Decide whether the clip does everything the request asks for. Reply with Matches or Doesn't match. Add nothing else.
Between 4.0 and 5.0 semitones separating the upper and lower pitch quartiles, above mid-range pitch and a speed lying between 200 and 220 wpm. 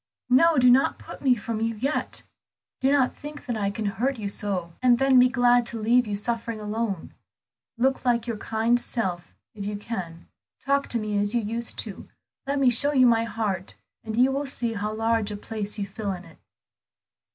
Doesn't match